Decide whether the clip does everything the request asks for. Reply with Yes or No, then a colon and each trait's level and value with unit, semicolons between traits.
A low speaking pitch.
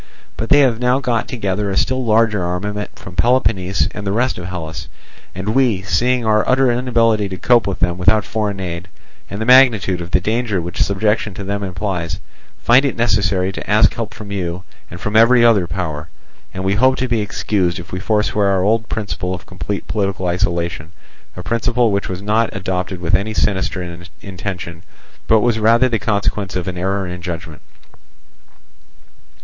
Yes: low, 100 Hz